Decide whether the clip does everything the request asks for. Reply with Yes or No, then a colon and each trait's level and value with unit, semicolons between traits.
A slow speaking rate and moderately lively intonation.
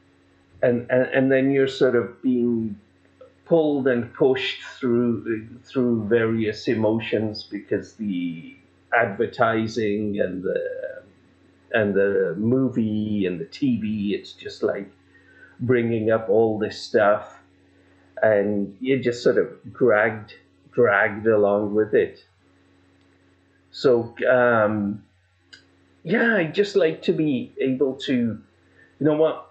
Yes: slow, 115 wpm; average, 4.9 semitones